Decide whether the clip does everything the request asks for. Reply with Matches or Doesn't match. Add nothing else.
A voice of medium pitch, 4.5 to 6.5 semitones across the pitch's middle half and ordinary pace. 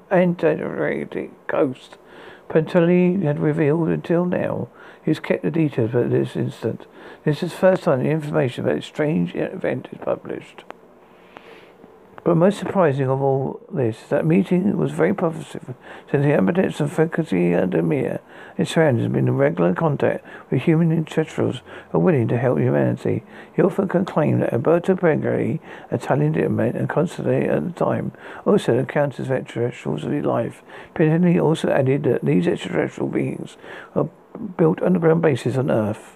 Matches